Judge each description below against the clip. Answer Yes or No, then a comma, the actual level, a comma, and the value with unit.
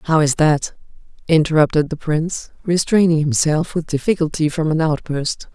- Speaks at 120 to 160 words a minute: Yes, average, 140 wpm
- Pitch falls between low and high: Yes, medium, 155 Hz